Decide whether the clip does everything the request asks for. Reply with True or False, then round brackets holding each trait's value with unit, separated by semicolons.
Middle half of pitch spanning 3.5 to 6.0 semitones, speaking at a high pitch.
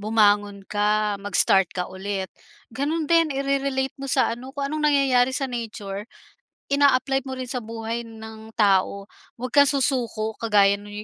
True (4.6 semitones; 230 Hz)